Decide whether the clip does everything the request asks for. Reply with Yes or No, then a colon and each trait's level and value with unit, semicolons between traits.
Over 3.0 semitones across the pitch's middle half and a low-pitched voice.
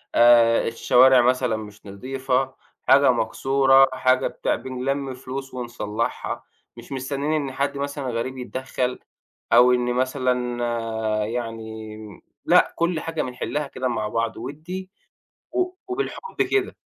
No: narrow, 2.6 semitones; low, 130 Hz